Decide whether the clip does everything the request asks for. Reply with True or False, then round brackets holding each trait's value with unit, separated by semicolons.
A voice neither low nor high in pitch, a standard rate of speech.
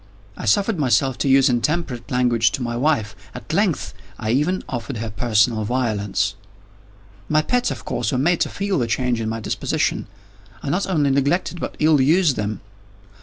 False (130 Hz; 175 wpm)